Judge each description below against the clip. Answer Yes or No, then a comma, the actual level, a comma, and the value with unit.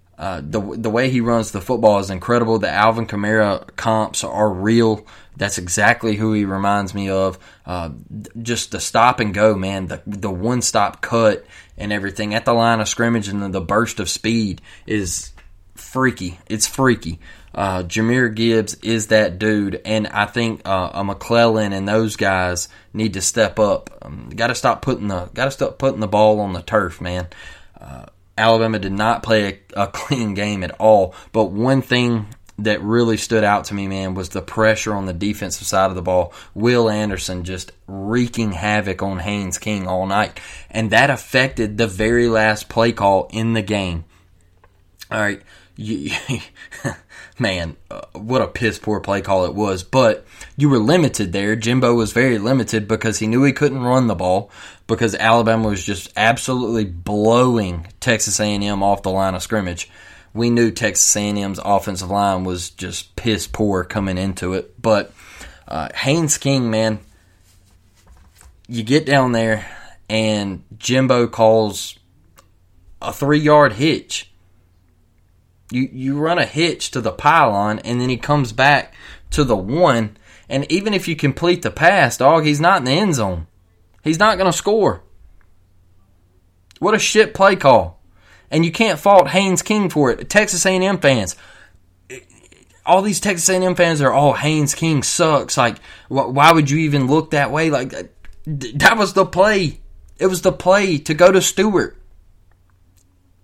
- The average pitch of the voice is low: Yes, low, 110 Hz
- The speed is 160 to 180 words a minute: Yes, average, 170 wpm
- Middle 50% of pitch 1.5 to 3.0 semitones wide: No, average, 4.5 semitones